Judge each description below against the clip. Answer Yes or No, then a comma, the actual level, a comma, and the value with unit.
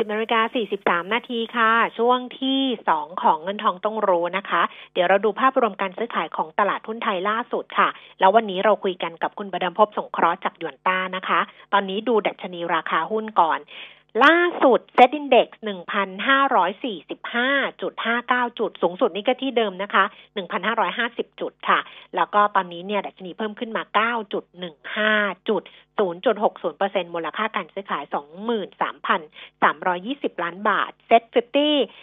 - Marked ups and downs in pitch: No, average, 3.7 semitones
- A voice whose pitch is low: No, high, 210 Hz